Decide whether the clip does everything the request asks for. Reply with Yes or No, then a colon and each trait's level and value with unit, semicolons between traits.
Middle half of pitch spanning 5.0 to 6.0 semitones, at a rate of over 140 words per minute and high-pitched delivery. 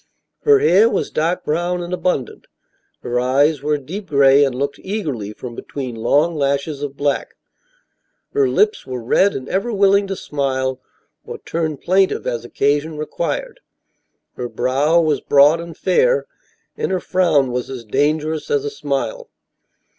No: wide, 5.5 semitones; average, 155 wpm; medium, 150 Hz